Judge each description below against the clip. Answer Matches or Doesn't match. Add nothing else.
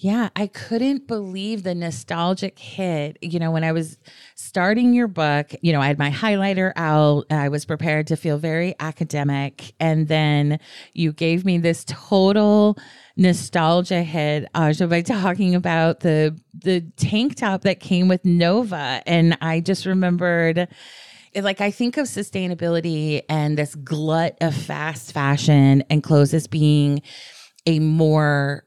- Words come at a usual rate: Matches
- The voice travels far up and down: Doesn't match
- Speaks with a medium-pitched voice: Matches